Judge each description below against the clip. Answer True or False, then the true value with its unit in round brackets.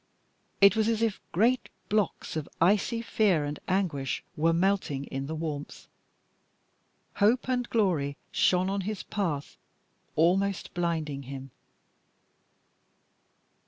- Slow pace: True (115 wpm)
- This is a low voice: False (180 Hz)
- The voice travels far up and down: True (5.7 semitones)